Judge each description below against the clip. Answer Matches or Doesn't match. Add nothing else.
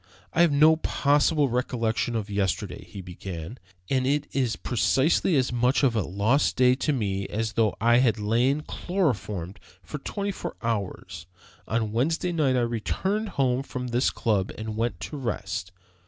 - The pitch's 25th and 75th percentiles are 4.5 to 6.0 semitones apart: Matches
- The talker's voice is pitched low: Matches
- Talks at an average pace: Matches